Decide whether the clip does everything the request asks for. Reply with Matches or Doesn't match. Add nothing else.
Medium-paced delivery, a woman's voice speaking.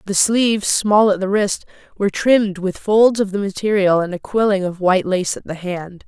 Doesn't match